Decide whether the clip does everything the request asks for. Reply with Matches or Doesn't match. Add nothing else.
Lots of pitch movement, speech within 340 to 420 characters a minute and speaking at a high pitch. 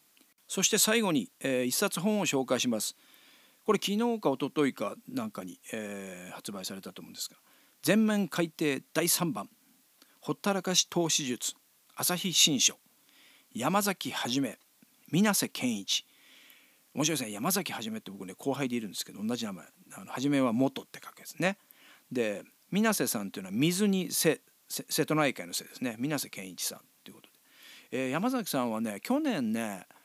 Doesn't match